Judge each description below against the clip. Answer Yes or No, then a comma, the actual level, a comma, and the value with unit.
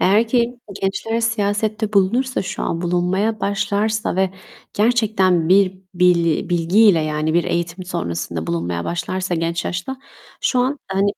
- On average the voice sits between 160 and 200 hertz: Yes, high, 190 Hz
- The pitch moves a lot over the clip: No, average, 4.1 semitones